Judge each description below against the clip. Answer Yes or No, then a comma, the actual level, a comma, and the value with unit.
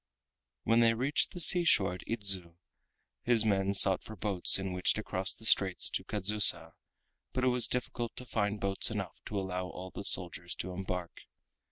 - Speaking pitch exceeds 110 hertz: No, low, 100 Hz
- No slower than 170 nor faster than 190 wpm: Yes, average, 180 wpm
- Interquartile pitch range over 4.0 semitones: No, average, 3.6 semitones